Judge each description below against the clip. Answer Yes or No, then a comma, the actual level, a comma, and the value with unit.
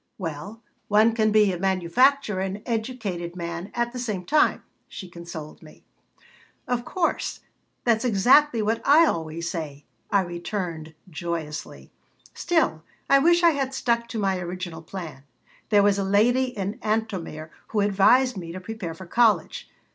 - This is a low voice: No, high, 200 Hz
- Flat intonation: No, wide, 5.4 semitones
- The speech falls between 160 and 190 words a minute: No, average, 150 wpm